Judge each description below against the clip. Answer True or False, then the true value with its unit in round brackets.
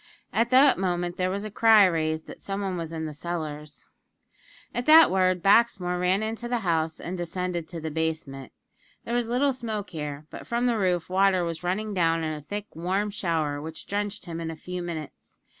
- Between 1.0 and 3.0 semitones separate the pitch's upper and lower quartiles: False (4.2 semitones)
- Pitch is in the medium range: True (180 Hz)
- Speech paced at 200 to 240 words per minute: True (205 wpm)